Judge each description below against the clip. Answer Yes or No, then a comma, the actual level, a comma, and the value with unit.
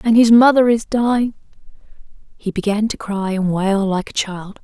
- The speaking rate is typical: Yes, average, 180 wpm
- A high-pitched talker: Yes, high, 210 Hz